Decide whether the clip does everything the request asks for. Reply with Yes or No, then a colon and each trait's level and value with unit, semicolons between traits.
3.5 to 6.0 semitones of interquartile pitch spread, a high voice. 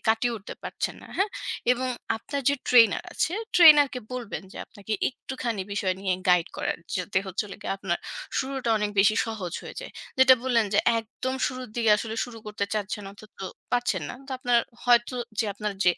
Yes: average, 3.9 semitones; high, 225 Hz